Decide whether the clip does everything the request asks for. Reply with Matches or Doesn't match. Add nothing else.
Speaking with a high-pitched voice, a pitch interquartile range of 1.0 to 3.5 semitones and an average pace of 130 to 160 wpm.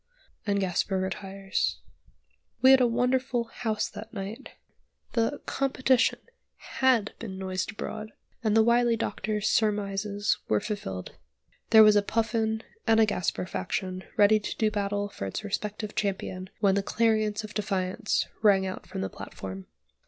Matches